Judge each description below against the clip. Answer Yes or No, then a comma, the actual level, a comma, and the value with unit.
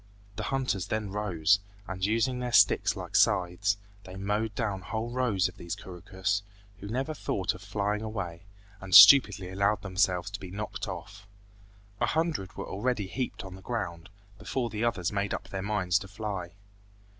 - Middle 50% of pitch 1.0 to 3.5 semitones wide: Yes, narrow, 2.6 semitones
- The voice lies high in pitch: No, low, 100 Hz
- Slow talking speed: No, average, 170 wpm